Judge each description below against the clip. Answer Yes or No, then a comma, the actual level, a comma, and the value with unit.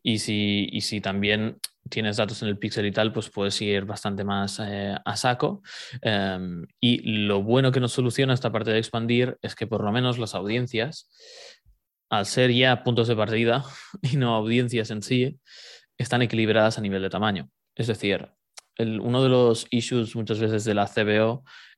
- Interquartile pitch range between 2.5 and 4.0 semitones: Yes, average, 3.0 semitones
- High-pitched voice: No, low, 110 Hz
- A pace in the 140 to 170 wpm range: No, average, 185 wpm